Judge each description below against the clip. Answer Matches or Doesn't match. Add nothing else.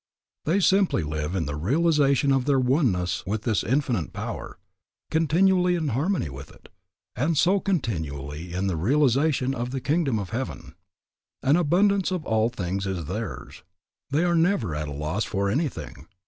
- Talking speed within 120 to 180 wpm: Matches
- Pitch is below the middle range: Matches